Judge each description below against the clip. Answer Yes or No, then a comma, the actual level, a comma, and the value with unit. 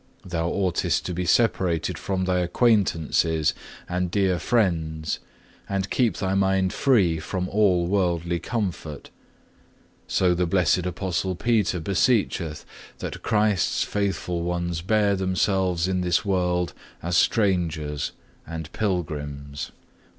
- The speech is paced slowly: Yes, slow, 115 wpm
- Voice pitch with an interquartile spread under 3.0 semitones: Yes, narrow, 2.5 semitones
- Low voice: Yes, very low, 90 Hz